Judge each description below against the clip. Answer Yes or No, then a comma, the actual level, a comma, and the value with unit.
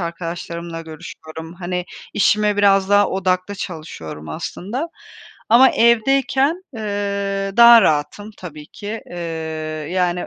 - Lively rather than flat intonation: No, average, 4.6 semitones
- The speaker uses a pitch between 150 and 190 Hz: Yes, medium, 185 Hz